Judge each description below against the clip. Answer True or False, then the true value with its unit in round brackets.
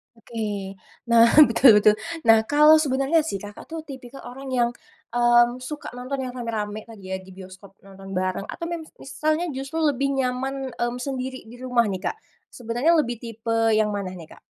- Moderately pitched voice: False (240 Hz)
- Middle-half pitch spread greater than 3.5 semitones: True (4.4 semitones)